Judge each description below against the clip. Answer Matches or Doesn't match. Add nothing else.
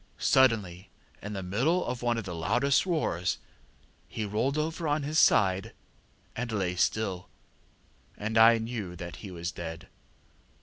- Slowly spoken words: Doesn't match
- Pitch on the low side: Matches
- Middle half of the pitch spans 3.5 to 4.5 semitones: Doesn't match